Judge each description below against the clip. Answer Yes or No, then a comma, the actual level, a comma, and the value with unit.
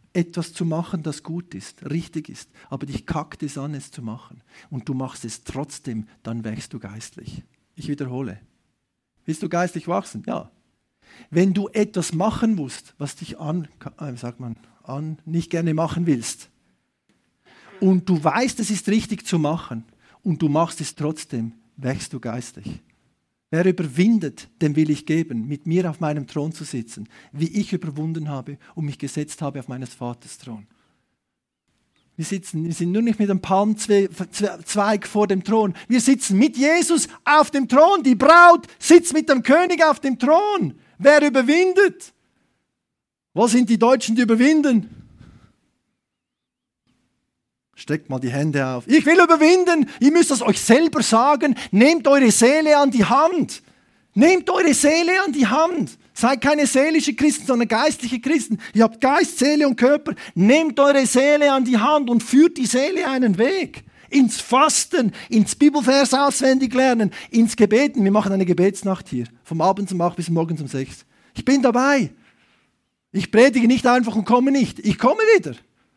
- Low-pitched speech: No, high, 205 Hz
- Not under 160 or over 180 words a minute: Yes, average, 165 wpm